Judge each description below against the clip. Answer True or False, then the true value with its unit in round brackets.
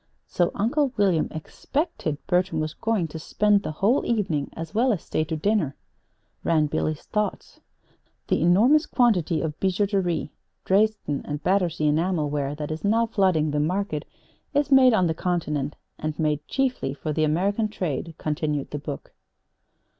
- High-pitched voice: False (175 Hz)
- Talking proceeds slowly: False (155 wpm)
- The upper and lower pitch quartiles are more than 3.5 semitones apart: True (5.4 semitones)